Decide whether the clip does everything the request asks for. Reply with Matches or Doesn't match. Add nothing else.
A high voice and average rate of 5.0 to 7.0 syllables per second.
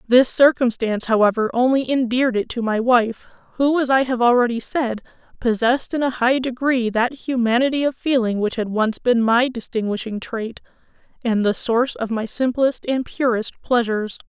Matches